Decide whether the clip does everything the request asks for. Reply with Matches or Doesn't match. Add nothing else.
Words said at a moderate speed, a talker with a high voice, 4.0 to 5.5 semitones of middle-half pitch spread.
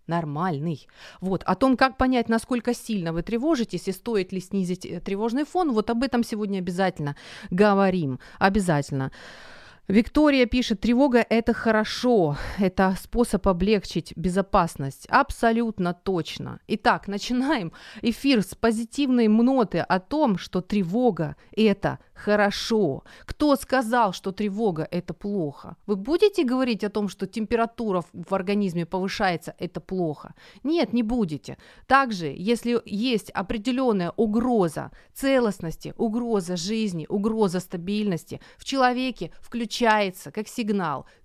Matches